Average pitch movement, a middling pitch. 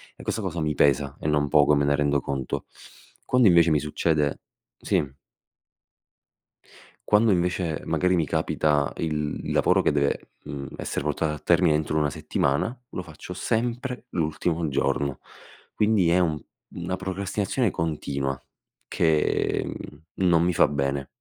No: average, 3.8 semitones; very low, 80 Hz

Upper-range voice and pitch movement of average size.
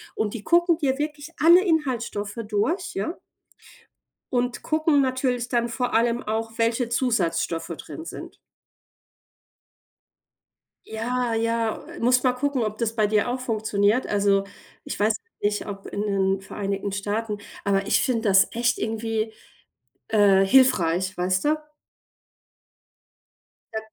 Yes: high, 225 Hz; average, 3.7 semitones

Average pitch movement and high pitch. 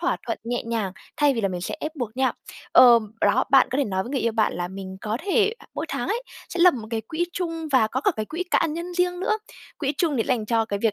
No: wide, 7.1 semitones; very high, 250 Hz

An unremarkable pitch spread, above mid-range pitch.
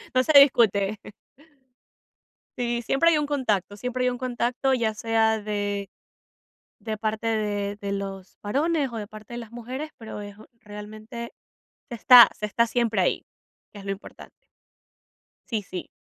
Yes: average, 3.2 semitones; high, 220 Hz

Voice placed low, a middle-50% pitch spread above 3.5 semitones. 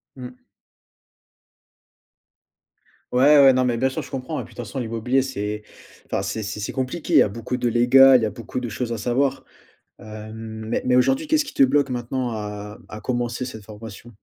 No: low, 120 Hz; average, 3.1 semitones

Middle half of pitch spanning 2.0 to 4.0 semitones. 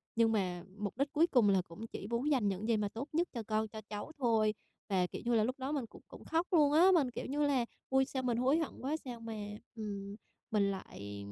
No: average, 4.8 semitones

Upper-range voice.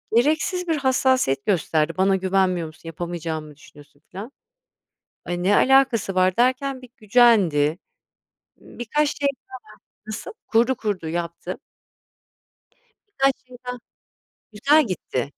Yes: high, 205 Hz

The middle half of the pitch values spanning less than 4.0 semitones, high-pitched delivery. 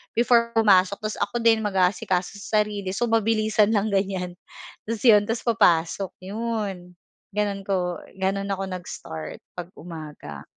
Yes: average, 3.2 semitones; high, 200 Hz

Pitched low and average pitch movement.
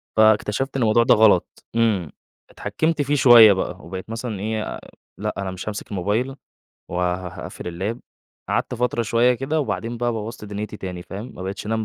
Yes: low, 110 Hz; average, 3.8 semitones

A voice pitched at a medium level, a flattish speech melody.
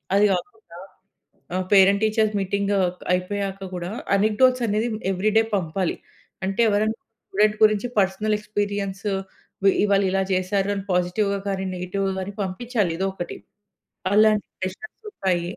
No: high, 200 Hz; narrow, 2.0 semitones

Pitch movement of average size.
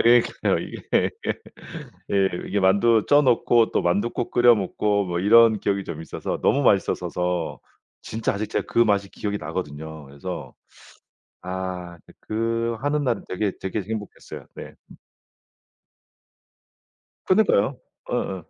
Yes: average, 4.2 semitones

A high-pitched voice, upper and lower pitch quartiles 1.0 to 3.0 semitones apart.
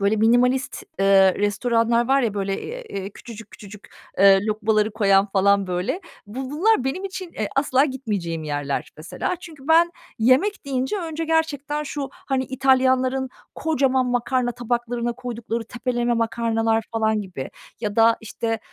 No: high, 240 Hz; average, 4.1 semitones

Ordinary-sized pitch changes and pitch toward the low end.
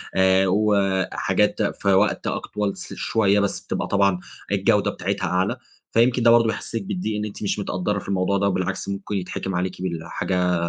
No: narrow, 1.9 semitones; low, 100 Hz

